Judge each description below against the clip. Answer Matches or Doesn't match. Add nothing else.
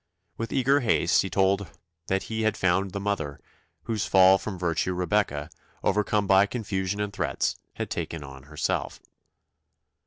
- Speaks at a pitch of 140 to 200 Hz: Doesn't match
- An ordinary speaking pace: Matches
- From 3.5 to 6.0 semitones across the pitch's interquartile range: Doesn't match